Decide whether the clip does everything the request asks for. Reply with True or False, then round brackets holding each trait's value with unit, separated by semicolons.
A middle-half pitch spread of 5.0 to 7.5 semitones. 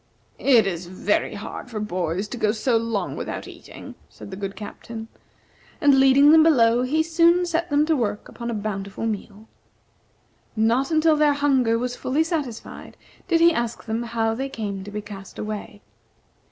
True (5.5 semitones)